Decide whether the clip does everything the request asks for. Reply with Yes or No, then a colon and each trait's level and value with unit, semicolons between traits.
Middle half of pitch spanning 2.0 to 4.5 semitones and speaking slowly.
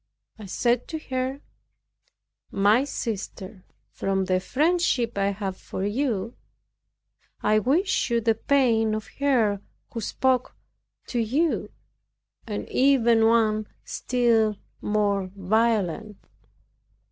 Yes: average, 3.7 semitones; slow, 105 wpm